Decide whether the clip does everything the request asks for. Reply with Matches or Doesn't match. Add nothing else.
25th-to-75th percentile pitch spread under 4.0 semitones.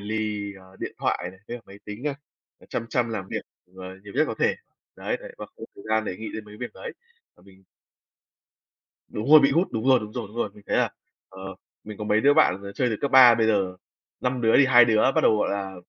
Matches